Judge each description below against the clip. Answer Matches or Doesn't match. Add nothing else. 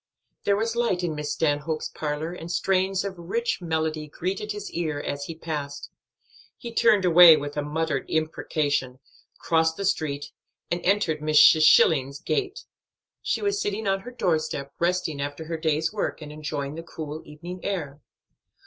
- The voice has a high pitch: Doesn't match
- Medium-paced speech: Matches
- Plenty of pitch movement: Doesn't match